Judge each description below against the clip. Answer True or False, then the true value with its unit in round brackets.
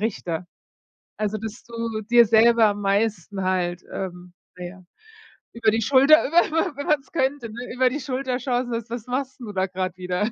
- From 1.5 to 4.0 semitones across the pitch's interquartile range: False (4.8 semitones)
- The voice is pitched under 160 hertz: False (225 Hz)